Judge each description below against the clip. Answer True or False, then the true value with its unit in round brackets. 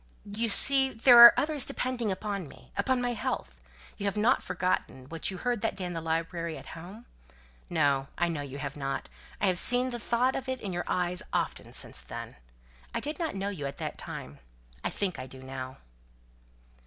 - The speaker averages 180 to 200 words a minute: True (190 wpm)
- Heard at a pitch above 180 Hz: True (190 Hz)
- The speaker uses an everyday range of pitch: False (7.3 semitones)